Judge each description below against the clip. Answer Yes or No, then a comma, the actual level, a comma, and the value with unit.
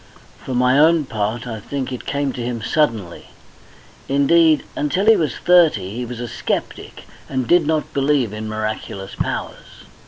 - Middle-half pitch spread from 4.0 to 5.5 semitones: Yes, average, 5.2 semitones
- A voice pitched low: Yes, low, 130 Hz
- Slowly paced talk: No, average, 160 wpm